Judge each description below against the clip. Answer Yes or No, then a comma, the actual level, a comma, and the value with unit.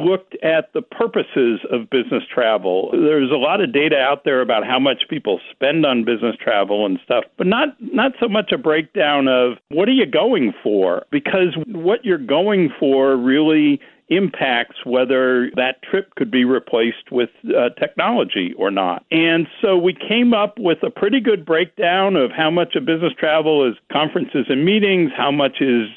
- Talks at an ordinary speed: Yes, average, 180 wpm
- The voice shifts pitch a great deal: Yes, wide, 6.4 semitones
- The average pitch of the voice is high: No, medium, 155 Hz